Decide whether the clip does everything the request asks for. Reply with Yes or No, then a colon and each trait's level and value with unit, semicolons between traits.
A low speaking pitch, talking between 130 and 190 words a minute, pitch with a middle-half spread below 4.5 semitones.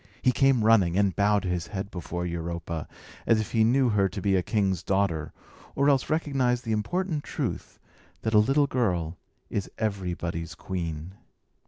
No: low, 100 Hz; average, 165 wpm; wide, 5.5 semitones